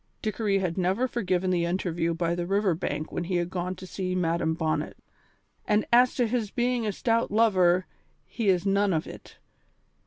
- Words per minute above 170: Yes, average, 185 wpm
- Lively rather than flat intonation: No, average, 3.5 semitones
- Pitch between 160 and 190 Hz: Yes, medium, 185 Hz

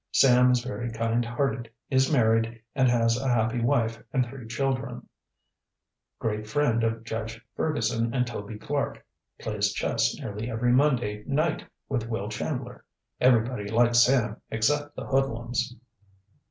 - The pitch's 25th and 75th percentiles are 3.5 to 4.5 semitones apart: No, narrow, 2.4 semitones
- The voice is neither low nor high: No, low, 120 Hz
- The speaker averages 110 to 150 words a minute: Yes, average, 140 wpm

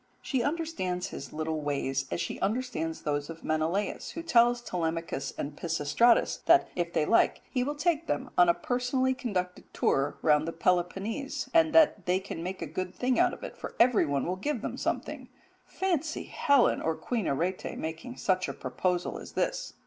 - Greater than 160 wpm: Yes, average, 180 wpm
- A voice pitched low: No, medium, 185 Hz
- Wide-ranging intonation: Yes, wide, 8.0 semitones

